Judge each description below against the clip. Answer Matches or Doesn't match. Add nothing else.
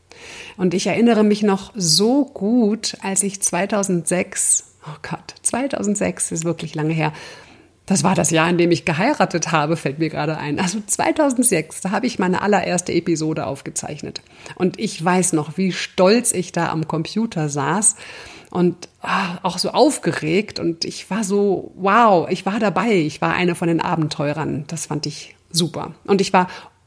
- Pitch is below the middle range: Doesn't match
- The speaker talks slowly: Doesn't match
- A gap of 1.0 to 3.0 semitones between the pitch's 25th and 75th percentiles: Doesn't match